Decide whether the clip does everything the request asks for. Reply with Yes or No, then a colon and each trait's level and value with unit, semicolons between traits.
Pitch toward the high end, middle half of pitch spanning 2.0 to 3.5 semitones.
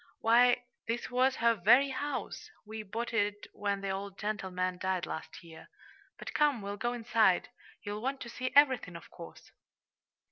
No: high, 220 Hz; average, 4.0 semitones